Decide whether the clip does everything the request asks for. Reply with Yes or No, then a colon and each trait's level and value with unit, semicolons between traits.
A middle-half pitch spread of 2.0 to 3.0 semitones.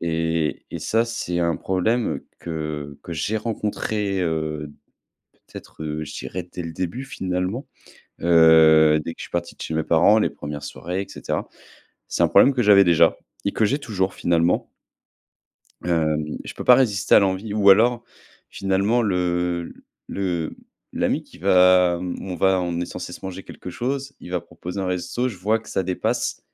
No: average, 3.6 semitones